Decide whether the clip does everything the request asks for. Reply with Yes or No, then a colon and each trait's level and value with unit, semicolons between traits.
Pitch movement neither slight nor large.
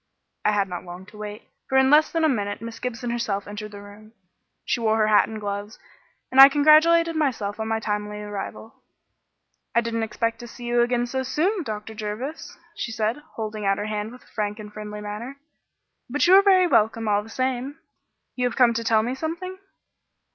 Yes: average, 3.9 semitones